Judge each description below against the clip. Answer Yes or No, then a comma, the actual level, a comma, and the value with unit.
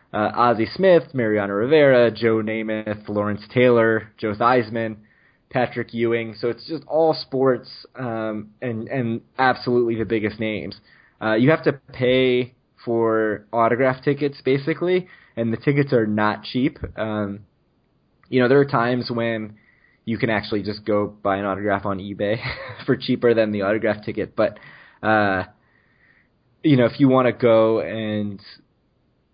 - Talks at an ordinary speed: Yes, average, 150 wpm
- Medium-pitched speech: No, low, 115 Hz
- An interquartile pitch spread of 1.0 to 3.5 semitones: Yes, average, 3.2 semitones